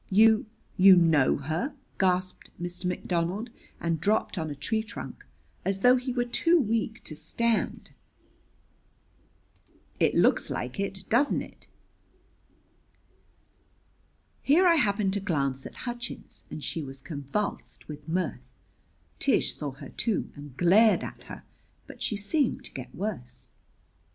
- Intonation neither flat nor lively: No, wide, 6.3 semitones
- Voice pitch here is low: No, high, 190 Hz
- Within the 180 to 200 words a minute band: No, slow, 135 wpm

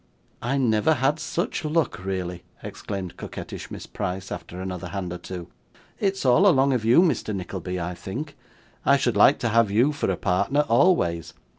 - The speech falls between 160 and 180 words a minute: Yes, average, 175 wpm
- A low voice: Yes, low, 115 Hz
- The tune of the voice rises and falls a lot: Yes, wide, 7.6 semitones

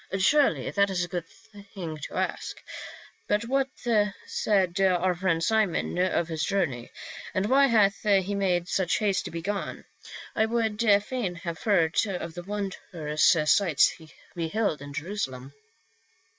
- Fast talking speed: No, average, 150 wpm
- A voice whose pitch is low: No, high, 190 Hz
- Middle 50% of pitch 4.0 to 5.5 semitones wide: No, average, 3.6 semitones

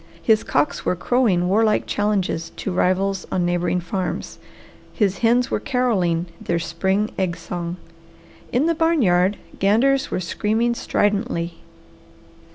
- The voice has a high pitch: Yes, high, 195 Hz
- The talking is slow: Yes, slow, 130 wpm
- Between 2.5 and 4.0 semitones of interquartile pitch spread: No, average, 4.7 semitones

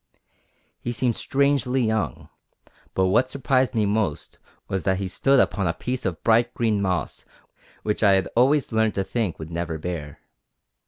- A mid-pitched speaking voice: No, low, 110 Hz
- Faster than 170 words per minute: No, average, 165 wpm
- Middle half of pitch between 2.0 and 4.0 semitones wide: No, average, 5.0 semitones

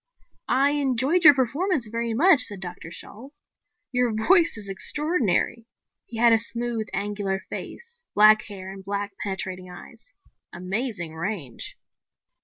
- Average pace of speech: No, slow, 130 wpm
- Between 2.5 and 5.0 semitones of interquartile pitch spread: No, wide, 5.4 semitones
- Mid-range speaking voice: No, high, 225 Hz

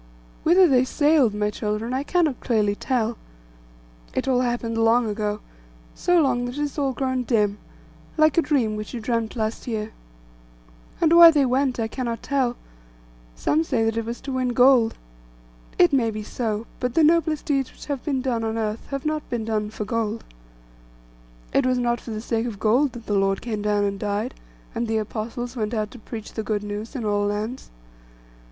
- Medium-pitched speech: No, high, 235 Hz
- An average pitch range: Yes, average, 3.6 semitones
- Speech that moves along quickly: No, average, 195 wpm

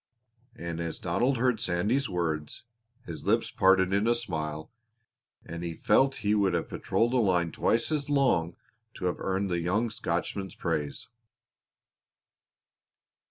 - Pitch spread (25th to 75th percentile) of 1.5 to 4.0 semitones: No, wide, 5.6 semitones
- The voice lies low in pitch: Yes, very low, 95 Hz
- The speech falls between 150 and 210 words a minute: No, average, 140 wpm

